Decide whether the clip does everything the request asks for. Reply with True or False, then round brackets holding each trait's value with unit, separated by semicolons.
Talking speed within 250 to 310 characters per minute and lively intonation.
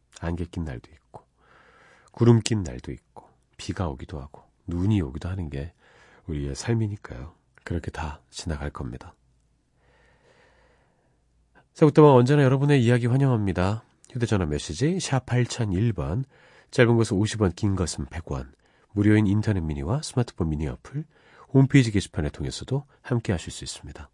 True (300 characters per minute; 7.9 semitones)